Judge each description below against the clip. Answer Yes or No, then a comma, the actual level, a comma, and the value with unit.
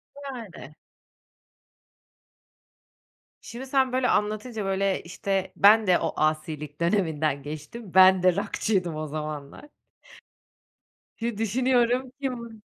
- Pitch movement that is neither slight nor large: No, wide, 6.9 semitones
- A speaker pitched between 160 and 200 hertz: Yes, high, 195 Hz